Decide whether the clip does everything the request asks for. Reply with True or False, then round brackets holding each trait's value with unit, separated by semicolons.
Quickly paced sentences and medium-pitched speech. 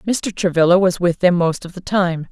True (235 wpm; 180 Hz)